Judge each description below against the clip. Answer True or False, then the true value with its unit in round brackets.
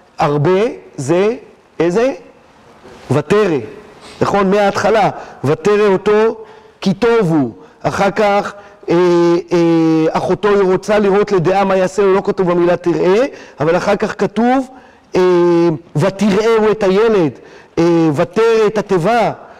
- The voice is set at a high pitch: True (195 Hz)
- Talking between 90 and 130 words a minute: True (120 wpm)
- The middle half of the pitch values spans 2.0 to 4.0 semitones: True (3.3 semitones)